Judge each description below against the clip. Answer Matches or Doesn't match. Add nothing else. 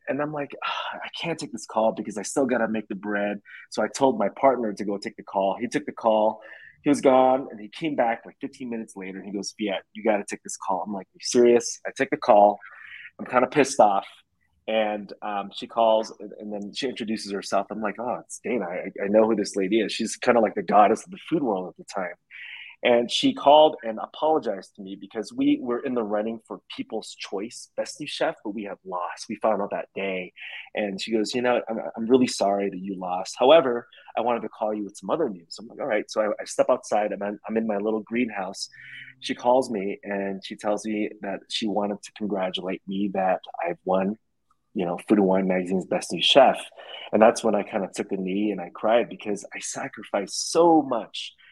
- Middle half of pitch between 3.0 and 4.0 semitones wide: Matches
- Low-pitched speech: Matches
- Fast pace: Matches